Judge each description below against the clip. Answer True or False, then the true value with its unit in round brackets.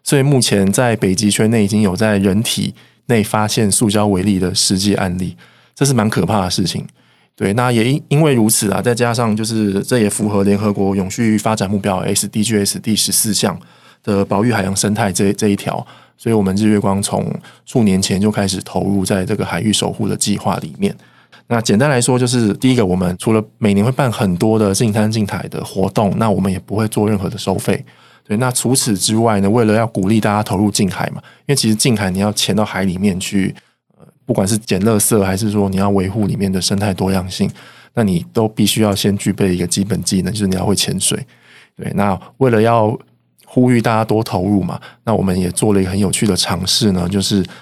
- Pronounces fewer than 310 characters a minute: False (320 characters per minute)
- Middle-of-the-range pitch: False (105 Hz)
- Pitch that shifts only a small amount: True (2.2 semitones)